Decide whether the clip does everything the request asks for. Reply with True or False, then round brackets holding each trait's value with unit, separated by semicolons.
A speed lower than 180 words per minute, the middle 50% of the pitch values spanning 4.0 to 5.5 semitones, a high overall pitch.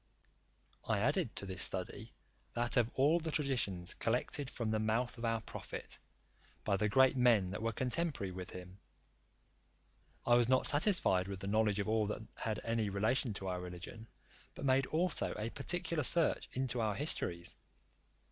False (165 wpm; 4.9 semitones; 115 Hz)